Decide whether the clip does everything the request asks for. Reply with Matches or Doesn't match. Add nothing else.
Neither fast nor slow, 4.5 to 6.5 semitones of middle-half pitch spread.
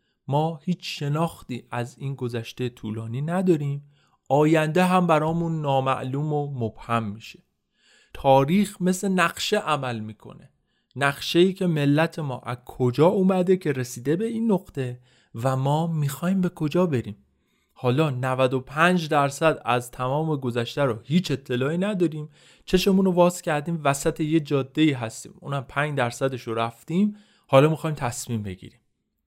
Matches